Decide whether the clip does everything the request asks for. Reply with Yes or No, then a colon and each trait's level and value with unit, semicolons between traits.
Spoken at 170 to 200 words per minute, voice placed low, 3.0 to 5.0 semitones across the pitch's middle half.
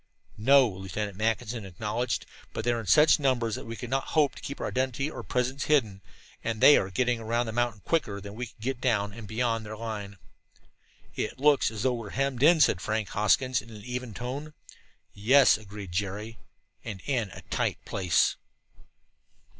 Yes: average, 190 wpm; low, 115 Hz; average, 3.6 semitones